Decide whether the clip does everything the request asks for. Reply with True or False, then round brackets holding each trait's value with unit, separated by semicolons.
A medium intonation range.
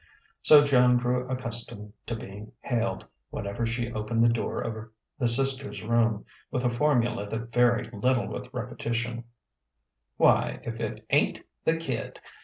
False (1.6 semitones)